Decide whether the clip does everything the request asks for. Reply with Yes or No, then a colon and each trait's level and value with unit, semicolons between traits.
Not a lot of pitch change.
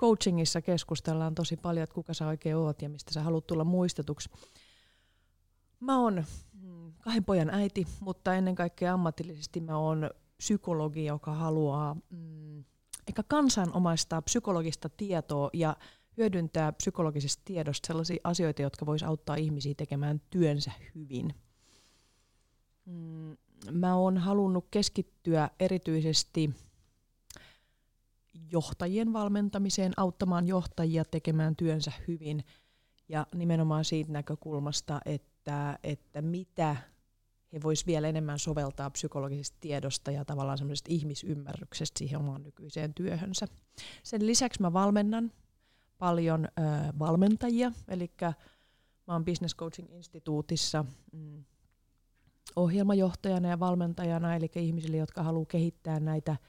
No: average, 3.2 semitones